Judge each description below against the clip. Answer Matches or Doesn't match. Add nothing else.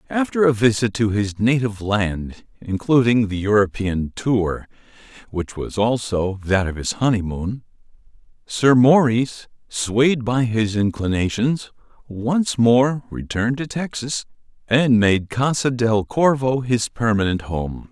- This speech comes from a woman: Doesn't match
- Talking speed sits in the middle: Doesn't match